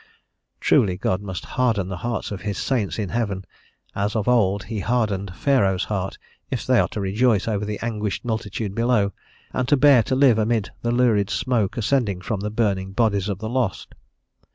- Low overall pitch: Yes, low, 105 Hz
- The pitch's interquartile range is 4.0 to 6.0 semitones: No, average, 3.3 semitones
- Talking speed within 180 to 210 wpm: Yes, average, 185 wpm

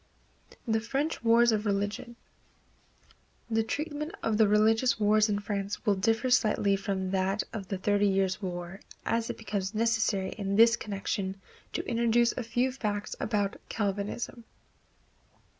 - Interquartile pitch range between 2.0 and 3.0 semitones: Yes, narrow, 2.5 semitones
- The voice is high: Yes, high, 210 Hz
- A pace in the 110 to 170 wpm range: Yes, average, 140 wpm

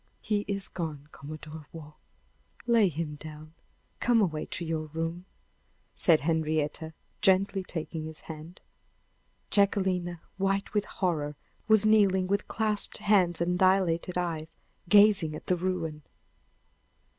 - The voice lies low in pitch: No, medium, 175 Hz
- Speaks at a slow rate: Yes, slow, 120 wpm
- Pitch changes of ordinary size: Yes, average, 3.8 semitones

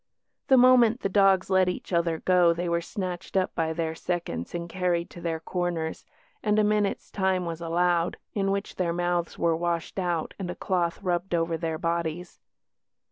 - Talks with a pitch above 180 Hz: No, medium, 175 Hz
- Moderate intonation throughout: No, narrow, 2.0 semitones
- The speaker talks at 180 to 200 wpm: Yes, average, 185 wpm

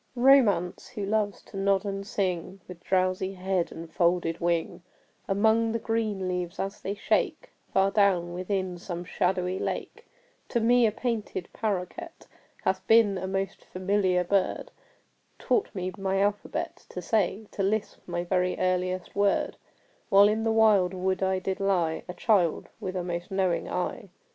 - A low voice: No, high, 190 Hz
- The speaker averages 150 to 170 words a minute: Yes, average, 160 wpm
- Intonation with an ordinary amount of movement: No, narrow, 2.2 semitones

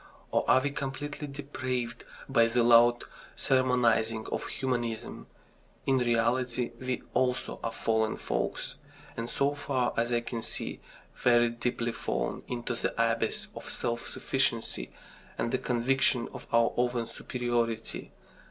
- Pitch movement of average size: No, narrow, 1.8 semitones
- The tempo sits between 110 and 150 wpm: Yes, slow, 135 wpm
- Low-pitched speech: Yes, low, 120 Hz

